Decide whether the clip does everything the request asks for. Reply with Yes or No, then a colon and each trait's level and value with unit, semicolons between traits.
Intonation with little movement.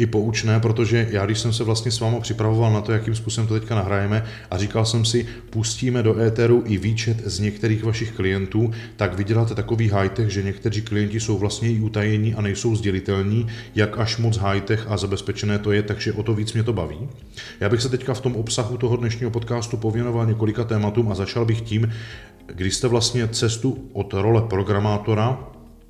Yes: narrow, 1.9 semitones